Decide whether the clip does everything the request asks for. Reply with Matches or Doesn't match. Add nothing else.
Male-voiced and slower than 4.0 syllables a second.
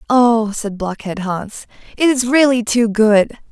Doesn't match